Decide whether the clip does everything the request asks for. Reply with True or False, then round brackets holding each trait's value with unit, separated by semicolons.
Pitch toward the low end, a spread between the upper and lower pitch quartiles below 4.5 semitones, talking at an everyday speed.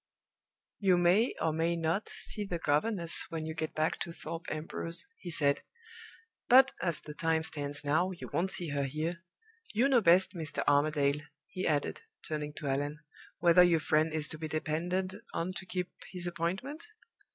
False (165 Hz; 2.8 semitones; 175 wpm)